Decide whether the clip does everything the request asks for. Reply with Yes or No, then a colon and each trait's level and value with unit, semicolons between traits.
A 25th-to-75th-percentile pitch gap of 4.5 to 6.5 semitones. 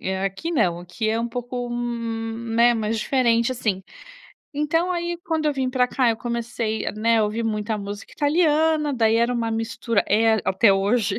No: average, 2.7 semitones